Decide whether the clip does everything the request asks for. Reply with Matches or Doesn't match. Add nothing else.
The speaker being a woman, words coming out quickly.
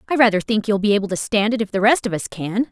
Matches